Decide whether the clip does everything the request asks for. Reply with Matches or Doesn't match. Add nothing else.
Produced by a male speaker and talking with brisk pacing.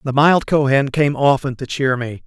Matches